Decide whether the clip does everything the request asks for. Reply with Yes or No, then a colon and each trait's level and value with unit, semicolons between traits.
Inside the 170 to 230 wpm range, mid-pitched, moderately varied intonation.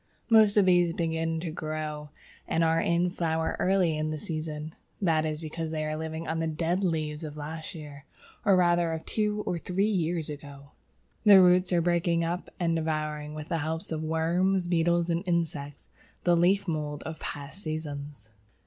No: average, 185 wpm; medium, 165 Hz; narrow, 2.2 semitones